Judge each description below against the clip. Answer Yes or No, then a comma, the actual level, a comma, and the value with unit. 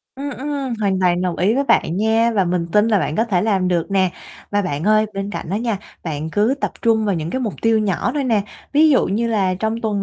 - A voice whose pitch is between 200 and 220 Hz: Yes, high, 210 Hz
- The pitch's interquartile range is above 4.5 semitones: No, average, 3.7 semitones